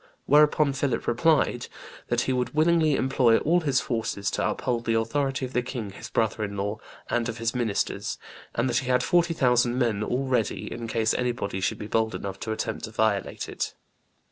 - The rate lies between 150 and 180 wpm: No, average, 195 wpm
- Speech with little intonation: No, average, 3.3 semitones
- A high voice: No, low, 120 Hz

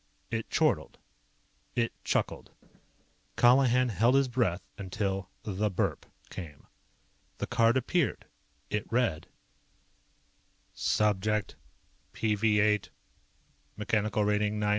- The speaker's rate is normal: No, slow, 90 wpm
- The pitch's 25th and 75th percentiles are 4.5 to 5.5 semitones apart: No, narrow, 2.5 semitones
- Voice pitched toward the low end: Yes, low, 105 Hz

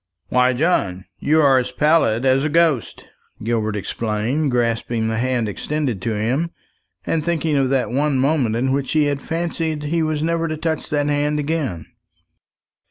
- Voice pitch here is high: No, medium, 140 Hz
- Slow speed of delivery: No, average, 165 wpm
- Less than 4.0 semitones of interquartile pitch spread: No, average, 4.8 semitones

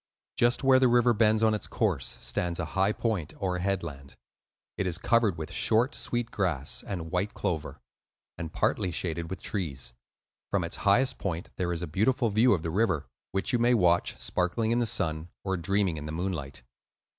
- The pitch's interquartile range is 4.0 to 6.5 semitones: Yes, average, 5.0 semitones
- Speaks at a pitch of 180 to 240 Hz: No, very low, 95 Hz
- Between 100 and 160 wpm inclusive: No, average, 190 wpm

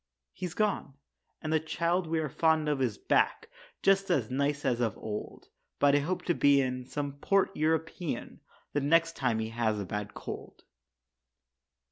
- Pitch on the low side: No, medium, 145 Hz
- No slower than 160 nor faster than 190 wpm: Yes, average, 170 wpm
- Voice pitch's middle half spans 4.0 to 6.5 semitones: Yes, average, 4.6 semitones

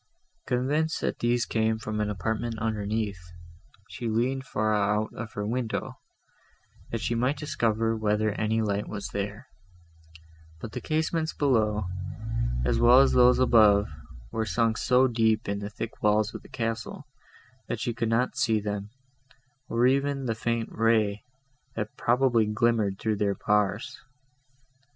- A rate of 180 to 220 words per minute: No, average, 145 wpm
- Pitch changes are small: Yes, narrow, 2.2 semitones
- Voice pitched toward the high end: No, low, 110 Hz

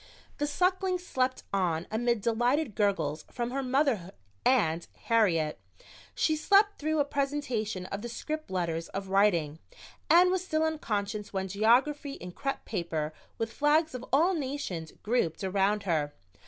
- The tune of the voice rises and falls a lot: Yes, wide, 7.5 semitones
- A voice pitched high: Yes, high, 230 Hz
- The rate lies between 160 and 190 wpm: No, average, 145 wpm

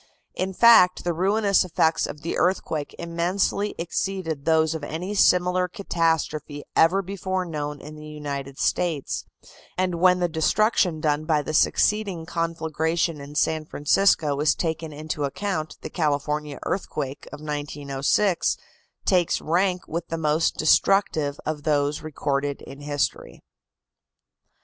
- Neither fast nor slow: No, slow, 130 wpm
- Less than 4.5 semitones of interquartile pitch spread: Yes, average, 3.4 semitones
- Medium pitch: Yes, medium, 160 Hz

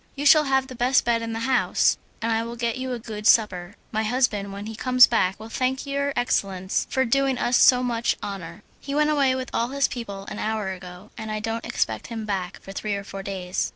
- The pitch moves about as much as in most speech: Yes, average, 4.1 semitones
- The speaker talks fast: Yes, fast, 235 wpm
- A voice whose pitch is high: Yes, high, 230 Hz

